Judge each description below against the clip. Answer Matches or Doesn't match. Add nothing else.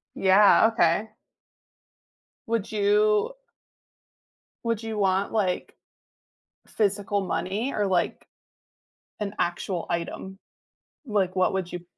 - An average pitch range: Doesn't match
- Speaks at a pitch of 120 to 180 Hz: Doesn't match